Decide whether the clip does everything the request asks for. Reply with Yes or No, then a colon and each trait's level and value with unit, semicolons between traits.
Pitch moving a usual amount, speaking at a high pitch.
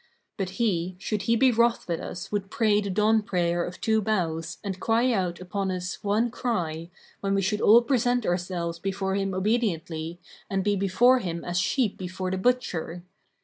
Yes: average, 3.6 semitones; high, 195 Hz